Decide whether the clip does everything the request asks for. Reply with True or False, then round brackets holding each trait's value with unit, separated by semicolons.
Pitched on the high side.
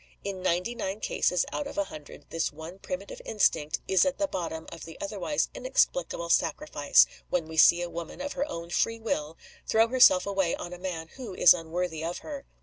False (180 Hz)